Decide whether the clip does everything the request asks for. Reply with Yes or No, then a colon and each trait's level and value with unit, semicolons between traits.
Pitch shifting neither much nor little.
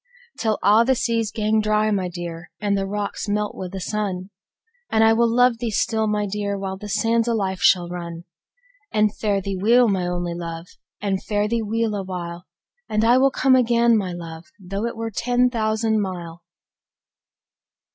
Yes: average, 3.2 semitones